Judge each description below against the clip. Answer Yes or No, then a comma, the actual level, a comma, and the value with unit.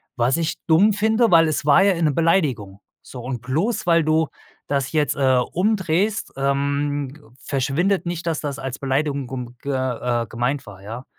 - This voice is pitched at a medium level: Yes, medium, 145 Hz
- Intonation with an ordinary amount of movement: Yes, average, 4.3 semitones